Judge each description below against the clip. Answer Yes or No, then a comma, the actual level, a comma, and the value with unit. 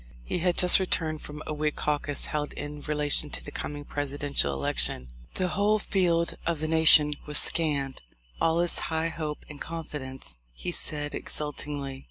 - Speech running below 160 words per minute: No, average, 165 wpm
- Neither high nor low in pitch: Yes, medium, 150 Hz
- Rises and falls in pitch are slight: Yes, narrow, 2.1 semitones